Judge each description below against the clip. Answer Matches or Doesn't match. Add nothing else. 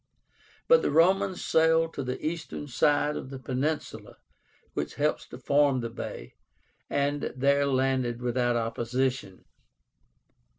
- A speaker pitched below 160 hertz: Matches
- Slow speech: Matches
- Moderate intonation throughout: Matches